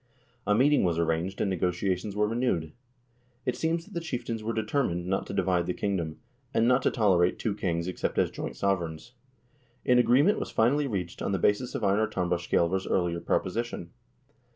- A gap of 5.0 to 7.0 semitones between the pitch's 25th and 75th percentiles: Yes, average, 5.3 semitones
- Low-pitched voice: Yes, low, 100 Hz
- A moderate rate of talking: Yes, average, 175 wpm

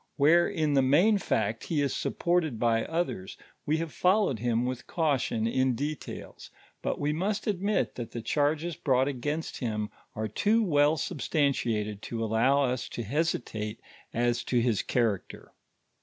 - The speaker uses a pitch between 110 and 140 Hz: Yes, low, 135 Hz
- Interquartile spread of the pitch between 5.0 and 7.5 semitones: Yes, wide, 5.5 semitones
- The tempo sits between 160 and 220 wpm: No, average, 150 wpm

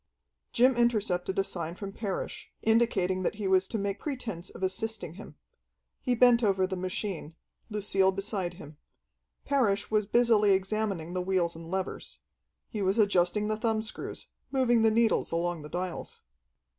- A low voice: No, high, 195 Hz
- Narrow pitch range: No, average, 3.2 semitones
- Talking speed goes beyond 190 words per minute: No, average, 155 wpm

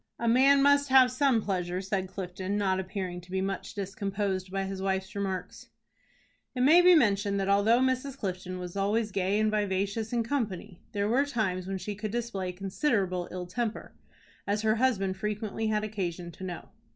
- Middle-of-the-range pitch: No, high, 200 Hz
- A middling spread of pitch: Yes, average, 3.3 semitones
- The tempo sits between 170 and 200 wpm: Yes, average, 180 wpm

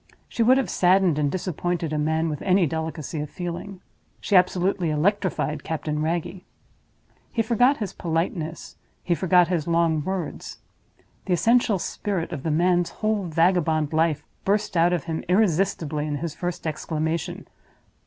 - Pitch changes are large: No, average, 3.0 semitones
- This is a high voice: No, medium, 170 Hz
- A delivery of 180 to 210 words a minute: No, average, 150 wpm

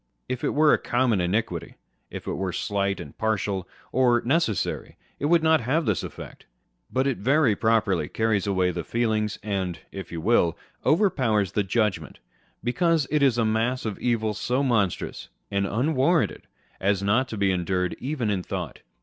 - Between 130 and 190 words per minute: Yes, average, 170 wpm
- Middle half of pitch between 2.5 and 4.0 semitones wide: No, average, 4.8 semitones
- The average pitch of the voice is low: Yes, low, 110 Hz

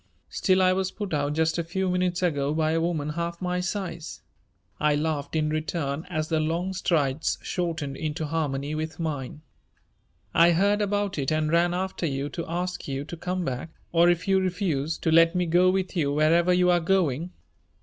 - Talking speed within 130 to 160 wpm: No, average, 190 wpm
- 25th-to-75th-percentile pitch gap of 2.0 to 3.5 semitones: Yes, average, 2.8 semitones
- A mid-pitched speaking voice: Yes, medium, 165 Hz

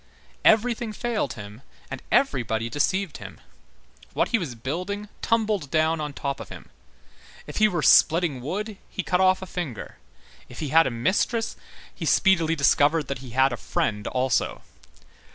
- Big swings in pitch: Yes, wide, 7.0 semitones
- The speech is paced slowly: No, average, 160 wpm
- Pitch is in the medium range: Yes, medium, 160 Hz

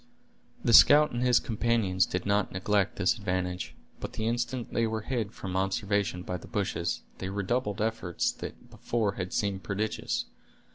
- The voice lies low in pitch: Yes, low, 100 Hz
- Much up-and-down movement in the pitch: No, average, 3.6 semitones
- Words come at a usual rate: Yes, average, 160 wpm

